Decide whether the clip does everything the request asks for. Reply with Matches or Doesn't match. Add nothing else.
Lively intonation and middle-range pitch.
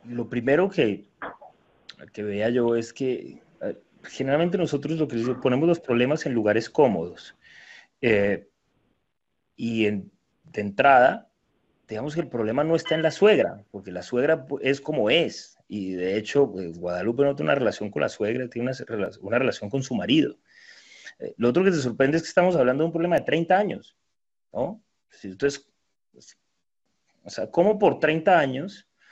Doesn't match